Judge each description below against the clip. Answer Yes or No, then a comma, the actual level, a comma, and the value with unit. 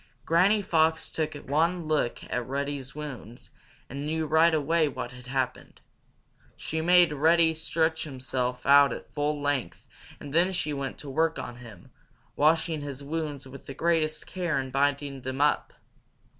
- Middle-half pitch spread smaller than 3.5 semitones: Yes, average, 2.9 semitones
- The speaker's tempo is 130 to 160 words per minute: Yes, average, 155 wpm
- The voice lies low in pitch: No, medium, 145 Hz